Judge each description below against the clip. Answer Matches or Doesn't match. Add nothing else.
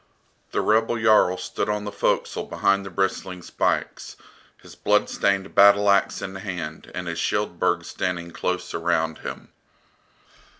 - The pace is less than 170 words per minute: Matches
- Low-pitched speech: Matches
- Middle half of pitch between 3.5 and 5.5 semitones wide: Doesn't match